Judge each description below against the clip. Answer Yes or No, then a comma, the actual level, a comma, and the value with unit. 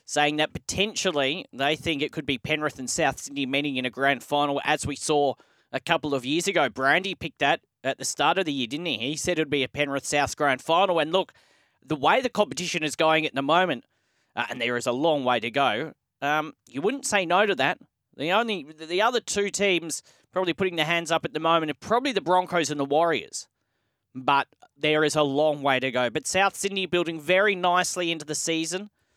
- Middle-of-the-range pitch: Yes, medium, 155 Hz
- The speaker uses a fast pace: Yes, fast, 230 wpm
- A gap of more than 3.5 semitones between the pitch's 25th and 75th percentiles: Yes, average, 3.9 semitones